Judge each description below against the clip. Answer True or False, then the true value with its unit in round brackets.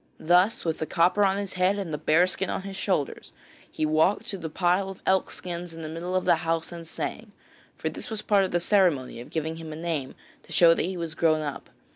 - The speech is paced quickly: True (245 wpm)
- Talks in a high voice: False (170 Hz)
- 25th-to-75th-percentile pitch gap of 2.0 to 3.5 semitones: True (2.9 semitones)